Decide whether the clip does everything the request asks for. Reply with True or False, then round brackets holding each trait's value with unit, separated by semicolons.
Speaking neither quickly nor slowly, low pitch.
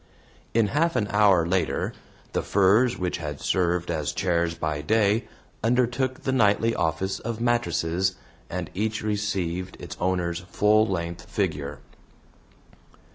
False (130 wpm; 95 Hz)